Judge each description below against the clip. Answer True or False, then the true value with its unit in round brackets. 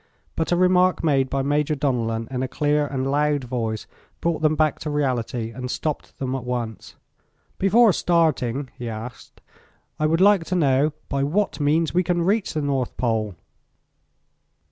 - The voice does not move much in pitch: False (4.4 semitones)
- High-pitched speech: False (145 Hz)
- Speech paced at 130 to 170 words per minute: True (165 wpm)